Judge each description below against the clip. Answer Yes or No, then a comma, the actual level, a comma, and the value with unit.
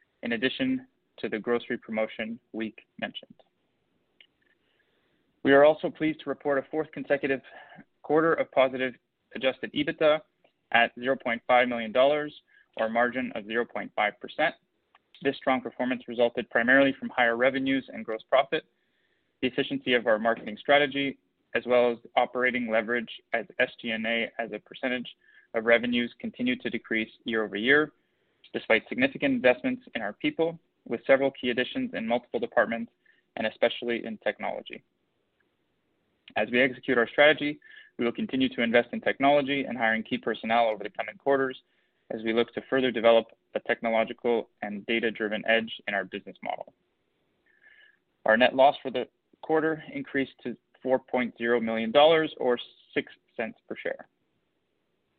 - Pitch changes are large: No, average, 3.6 semitones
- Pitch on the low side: Yes, low, 125 Hz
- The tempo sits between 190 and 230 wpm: No, average, 145 wpm